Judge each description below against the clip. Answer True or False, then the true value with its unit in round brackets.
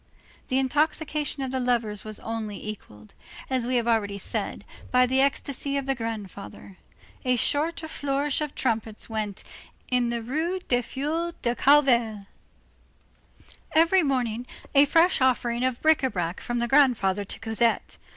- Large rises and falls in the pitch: False (4.0 semitones)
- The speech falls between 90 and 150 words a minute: False (160 wpm)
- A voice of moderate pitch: False (250 Hz)